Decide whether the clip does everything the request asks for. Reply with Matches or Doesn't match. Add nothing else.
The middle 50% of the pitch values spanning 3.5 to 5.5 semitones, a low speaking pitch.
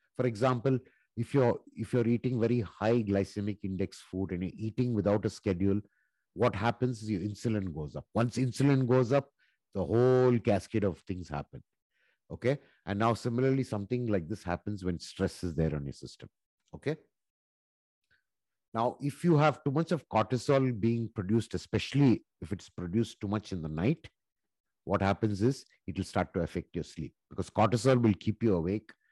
Matches